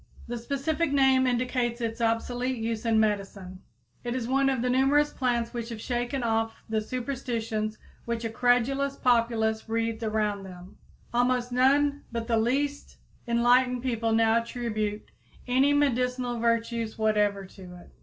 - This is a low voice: No, high, 235 Hz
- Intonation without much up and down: Yes, narrow, 2.3 semitones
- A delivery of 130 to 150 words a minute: Yes, average, 145 wpm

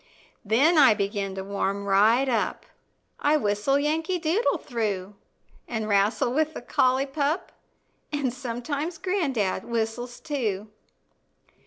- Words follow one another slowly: Yes, slow, 120 wpm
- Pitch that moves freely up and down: Yes, wide, 6.0 semitones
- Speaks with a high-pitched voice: Yes, high, 245 Hz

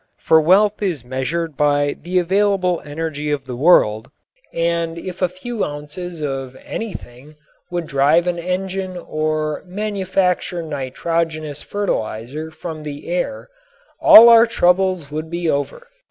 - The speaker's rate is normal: No, slow, 130 wpm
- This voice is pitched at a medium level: Yes, medium, 165 Hz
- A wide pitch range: No, average, 3.8 semitones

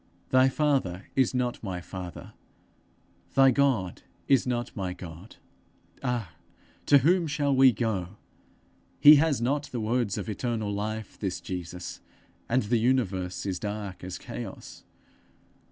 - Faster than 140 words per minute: No, slow, 135 wpm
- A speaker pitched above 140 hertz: No, low, 110 Hz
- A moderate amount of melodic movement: No, wide, 5.8 semitones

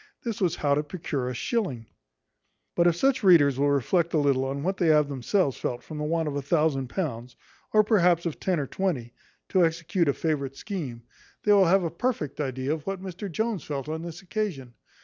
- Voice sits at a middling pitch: Yes, medium, 160 Hz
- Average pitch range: Yes, average, 5.0 semitones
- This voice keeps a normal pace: No, fast, 210 wpm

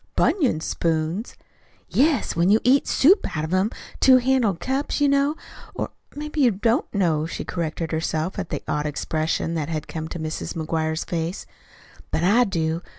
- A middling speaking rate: Yes, average, 170 wpm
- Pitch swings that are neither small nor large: No, wide, 8.0 semitones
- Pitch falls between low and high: Yes, medium, 175 Hz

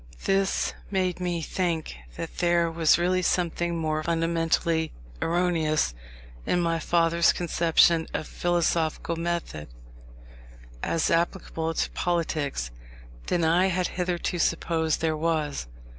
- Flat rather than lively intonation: Yes, narrow, 1.4 semitones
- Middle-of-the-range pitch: Yes, medium, 170 Hz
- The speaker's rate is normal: No, slow, 115 wpm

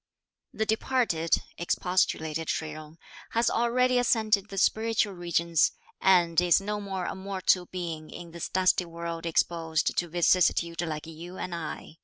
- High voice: No, medium, 175 Hz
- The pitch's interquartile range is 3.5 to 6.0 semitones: No, average, 3.1 semitones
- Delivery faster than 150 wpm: No, average, 145 wpm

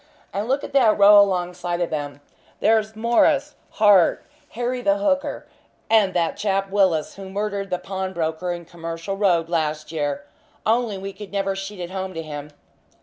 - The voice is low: No, high, 195 Hz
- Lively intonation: No, average, 3.6 semitones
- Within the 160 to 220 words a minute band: Yes, average, 165 wpm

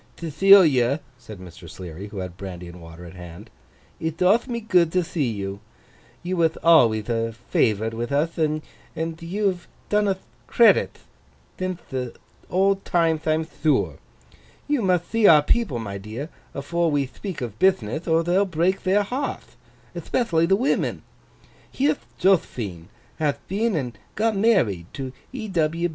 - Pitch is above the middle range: No, medium, 160 Hz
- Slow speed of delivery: No, average, 150 wpm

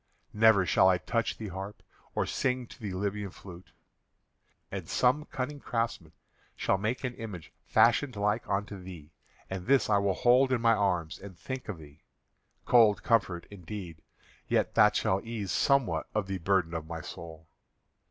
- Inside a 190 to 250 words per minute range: No, average, 165 wpm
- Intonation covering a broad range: No, average, 4.3 semitones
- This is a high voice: No, low, 100 Hz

